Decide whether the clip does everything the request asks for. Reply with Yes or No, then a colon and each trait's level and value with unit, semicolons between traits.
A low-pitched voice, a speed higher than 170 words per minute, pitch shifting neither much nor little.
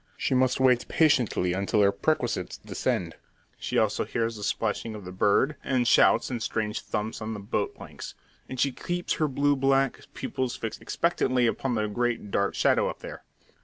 Yes: low, 120 Hz; average, 180 wpm; average, 3.9 semitones